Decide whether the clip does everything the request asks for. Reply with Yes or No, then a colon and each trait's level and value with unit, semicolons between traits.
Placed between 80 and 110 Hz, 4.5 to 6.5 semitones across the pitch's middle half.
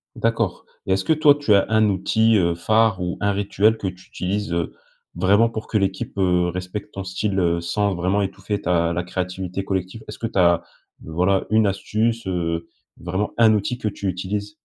No: very low, 95 Hz; average, 2.8 semitones